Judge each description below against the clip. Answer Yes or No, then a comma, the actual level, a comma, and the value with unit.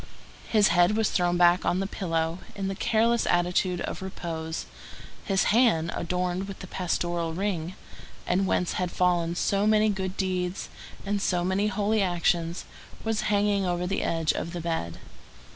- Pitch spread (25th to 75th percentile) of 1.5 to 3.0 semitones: Yes, narrow, 2.5 semitones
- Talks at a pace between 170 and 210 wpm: No, average, 160 wpm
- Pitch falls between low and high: Yes, medium, 180 Hz